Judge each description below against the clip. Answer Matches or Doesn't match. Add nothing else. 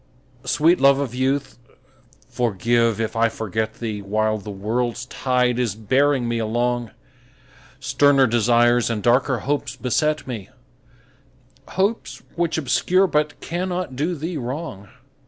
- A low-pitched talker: Matches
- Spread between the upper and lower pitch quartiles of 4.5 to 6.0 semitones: Doesn't match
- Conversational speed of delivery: Doesn't match